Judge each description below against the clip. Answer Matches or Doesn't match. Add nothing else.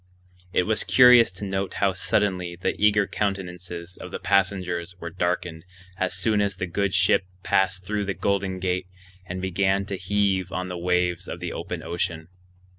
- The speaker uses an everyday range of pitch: Doesn't match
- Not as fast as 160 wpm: Doesn't match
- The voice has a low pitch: Matches